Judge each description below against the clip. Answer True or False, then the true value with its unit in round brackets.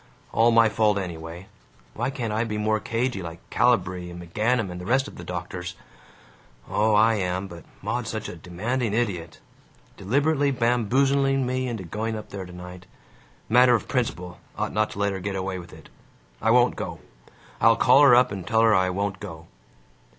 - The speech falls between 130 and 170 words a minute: False (185 wpm)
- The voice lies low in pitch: True (105 Hz)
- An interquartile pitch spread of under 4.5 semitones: False (5.0 semitones)